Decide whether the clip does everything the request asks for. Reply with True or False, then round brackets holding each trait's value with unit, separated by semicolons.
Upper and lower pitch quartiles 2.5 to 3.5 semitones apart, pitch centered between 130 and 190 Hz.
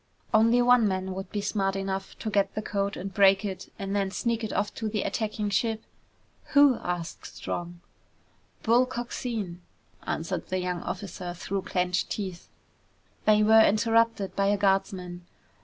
False (2.8 semitones; 200 Hz)